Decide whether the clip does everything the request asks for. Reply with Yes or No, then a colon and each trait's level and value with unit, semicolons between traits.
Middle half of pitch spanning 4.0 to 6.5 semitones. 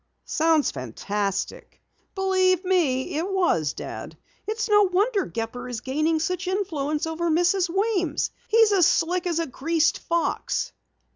Yes: average, 4.4 semitones